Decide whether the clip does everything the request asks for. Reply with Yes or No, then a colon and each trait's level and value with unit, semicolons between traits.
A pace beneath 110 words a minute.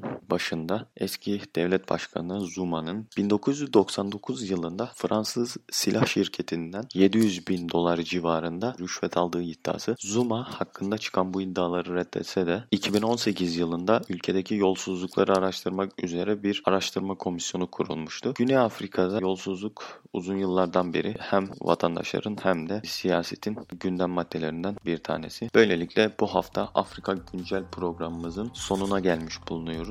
No: average, 115 wpm